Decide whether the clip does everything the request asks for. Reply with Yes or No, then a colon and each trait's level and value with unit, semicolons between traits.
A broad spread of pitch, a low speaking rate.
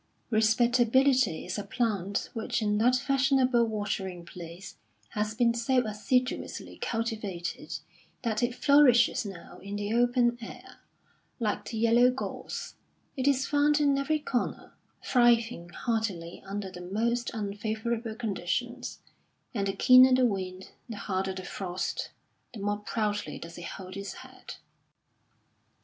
No: average, 3.8 semitones; slow, 130 wpm